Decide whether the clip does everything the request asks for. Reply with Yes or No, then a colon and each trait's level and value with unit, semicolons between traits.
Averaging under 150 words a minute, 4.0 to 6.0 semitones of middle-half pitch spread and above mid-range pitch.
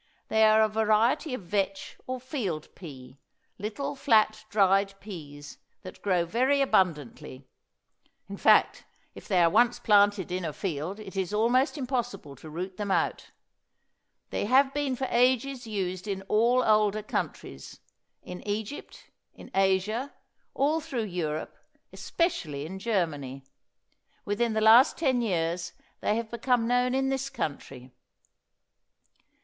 Yes: slow, 135 wpm; wide, 5.4 semitones; high, 210 Hz